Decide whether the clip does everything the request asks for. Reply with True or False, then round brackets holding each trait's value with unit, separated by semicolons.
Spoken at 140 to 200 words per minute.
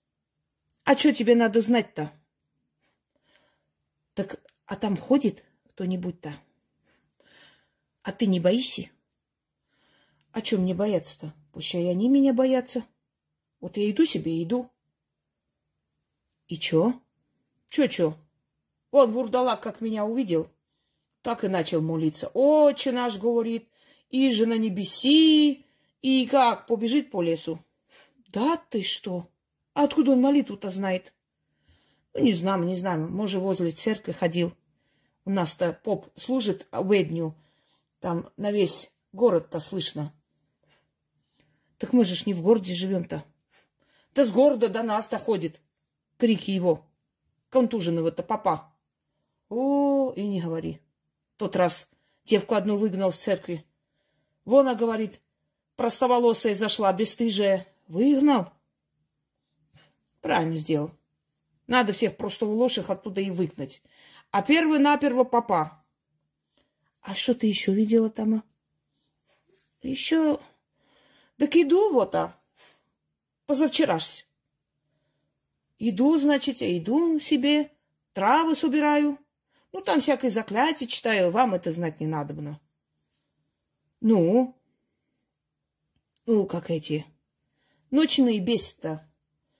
False (115 wpm)